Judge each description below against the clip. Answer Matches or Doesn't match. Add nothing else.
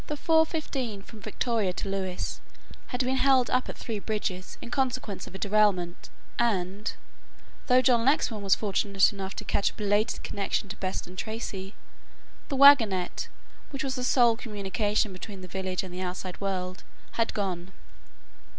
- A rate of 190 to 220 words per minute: Doesn't match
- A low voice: Doesn't match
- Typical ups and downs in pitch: Matches